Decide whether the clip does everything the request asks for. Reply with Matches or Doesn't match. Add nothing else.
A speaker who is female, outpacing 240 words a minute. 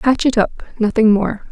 Doesn't match